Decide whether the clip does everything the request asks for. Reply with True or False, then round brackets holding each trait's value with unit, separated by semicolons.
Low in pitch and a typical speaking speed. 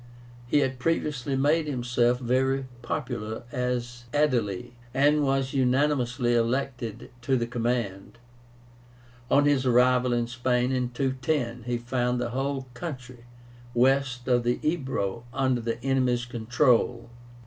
False (125 Hz; 125 wpm)